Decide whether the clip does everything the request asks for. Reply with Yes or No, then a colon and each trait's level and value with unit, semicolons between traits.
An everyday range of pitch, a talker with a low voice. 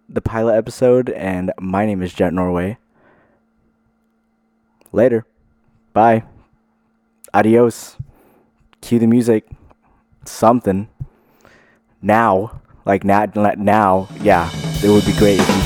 Yes: average, 3.5 semitones; low, 110 Hz